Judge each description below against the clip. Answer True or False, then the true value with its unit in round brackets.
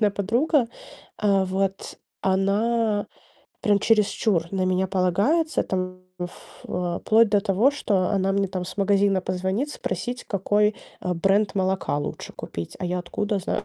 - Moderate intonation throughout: False (2.2 semitones)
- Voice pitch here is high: True (195 Hz)